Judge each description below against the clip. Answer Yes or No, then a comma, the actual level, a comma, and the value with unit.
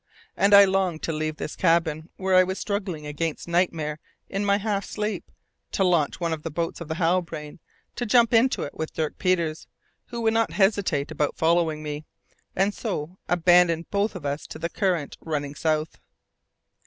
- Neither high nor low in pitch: Yes, medium, 170 Hz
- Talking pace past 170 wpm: Yes, average, 180 wpm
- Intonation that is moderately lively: Yes, average, 3.9 semitones